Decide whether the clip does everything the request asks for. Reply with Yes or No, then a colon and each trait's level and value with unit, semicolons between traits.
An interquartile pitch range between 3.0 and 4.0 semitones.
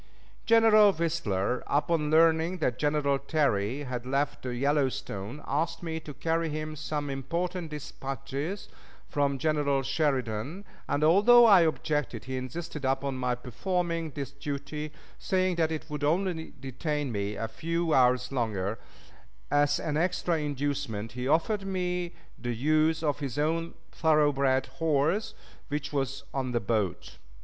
Yes: average, 3.6 semitones